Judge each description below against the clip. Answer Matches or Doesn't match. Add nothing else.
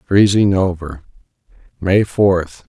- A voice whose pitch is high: Doesn't match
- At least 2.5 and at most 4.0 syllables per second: Matches